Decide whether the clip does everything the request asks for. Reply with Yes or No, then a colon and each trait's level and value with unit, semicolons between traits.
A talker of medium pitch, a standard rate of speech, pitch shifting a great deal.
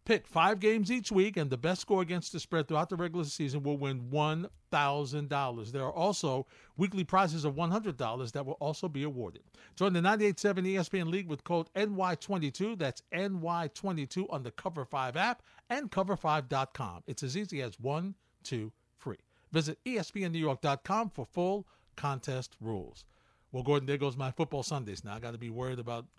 Yes: medium, 155 Hz; average, 180 wpm; wide, 5.8 semitones